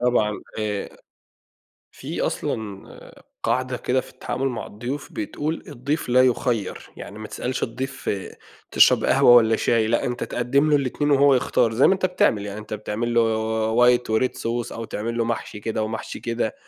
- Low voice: Yes, low, 120 Hz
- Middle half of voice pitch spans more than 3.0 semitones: No, average, 2.7 semitones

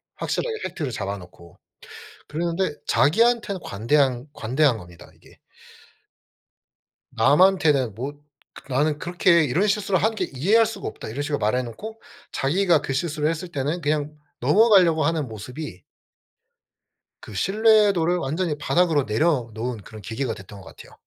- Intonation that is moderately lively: No, wide, 6.3 semitones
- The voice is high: No, medium, 150 Hz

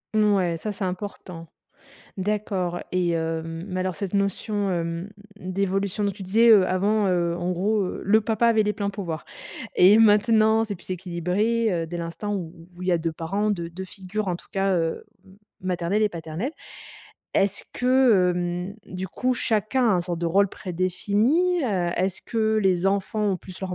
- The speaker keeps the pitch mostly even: No, average, 3.1 semitones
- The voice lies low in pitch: No, high, 190 Hz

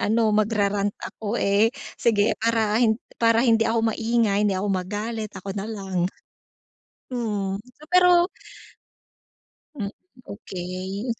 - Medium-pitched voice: No, high, 215 Hz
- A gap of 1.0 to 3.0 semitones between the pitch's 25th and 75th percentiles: Yes, narrow, 2.4 semitones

